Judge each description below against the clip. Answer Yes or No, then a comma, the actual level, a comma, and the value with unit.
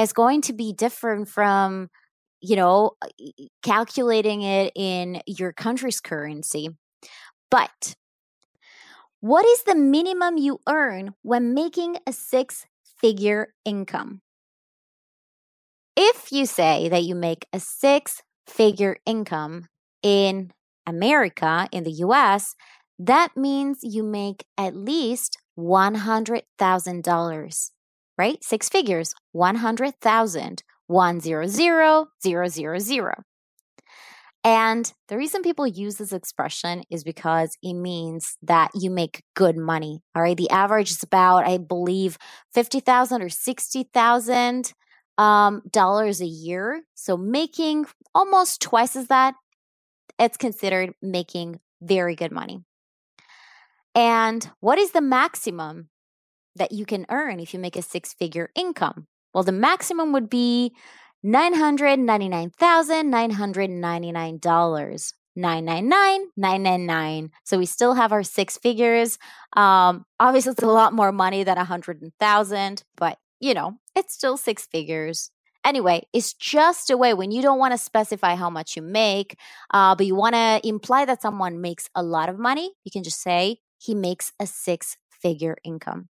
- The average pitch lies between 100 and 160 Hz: No, high, 205 Hz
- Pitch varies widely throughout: Yes, wide, 5.7 semitones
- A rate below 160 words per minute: Yes, average, 140 wpm